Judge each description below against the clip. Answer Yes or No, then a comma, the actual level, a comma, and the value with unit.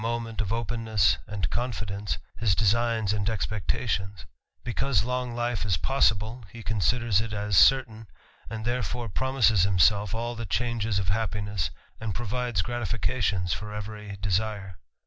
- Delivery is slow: Yes, slow, 125 wpm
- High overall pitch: No, low, 110 Hz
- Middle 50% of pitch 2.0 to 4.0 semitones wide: Yes, average, 2.7 semitones